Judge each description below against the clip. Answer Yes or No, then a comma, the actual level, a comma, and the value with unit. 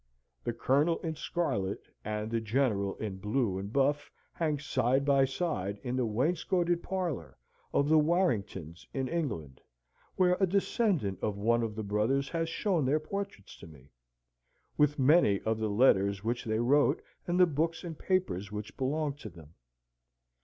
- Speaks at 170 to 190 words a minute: No, average, 160 wpm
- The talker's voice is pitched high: No, low, 130 Hz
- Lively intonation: Yes, wide, 7.5 semitones